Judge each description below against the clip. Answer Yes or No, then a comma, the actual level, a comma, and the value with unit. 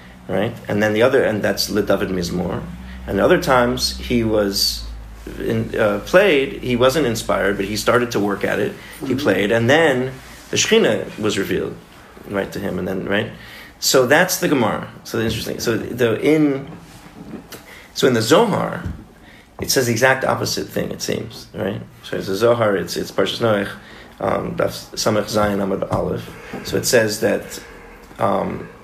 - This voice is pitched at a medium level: No, low, 115 Hz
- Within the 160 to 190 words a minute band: Yes, average, 165 wpm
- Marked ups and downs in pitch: No, average, 4.4 semitones